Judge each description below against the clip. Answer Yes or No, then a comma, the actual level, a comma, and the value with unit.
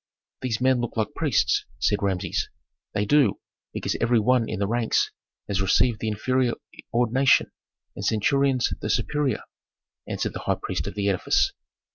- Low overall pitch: Yes, low, 115 Hz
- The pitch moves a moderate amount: Yes, average, 3.7 semitones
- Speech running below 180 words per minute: Yes, average, 155 wpm